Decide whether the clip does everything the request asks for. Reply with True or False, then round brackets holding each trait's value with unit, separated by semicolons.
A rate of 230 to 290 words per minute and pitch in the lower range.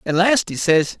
False (240 wpm; 190 Hz)